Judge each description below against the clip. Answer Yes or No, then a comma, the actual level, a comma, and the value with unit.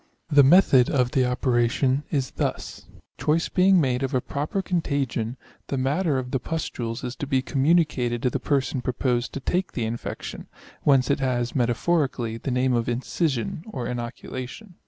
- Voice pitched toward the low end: Yes, low, 130 Hz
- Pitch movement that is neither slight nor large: Yes, average, 3.0 semitones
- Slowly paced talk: No, average, 170 wpm